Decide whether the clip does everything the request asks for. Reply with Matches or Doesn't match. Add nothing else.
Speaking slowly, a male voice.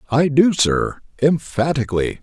Matches